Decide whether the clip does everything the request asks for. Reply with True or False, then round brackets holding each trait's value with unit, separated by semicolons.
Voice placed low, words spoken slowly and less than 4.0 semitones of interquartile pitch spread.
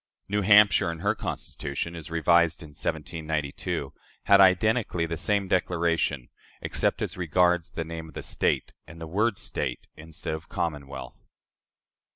False (85 Hz; 145 wpm; 2.7 semitones)